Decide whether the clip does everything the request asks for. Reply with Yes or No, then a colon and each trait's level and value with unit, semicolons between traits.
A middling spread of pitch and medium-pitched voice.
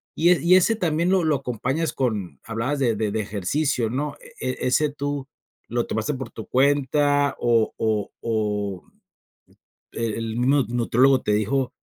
No: average, 4.5 semitones; low, 125 Hz